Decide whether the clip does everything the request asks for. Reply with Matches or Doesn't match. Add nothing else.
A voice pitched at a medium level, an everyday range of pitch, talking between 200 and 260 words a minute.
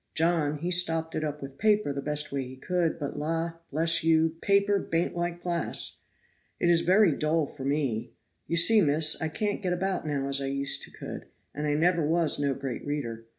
Matches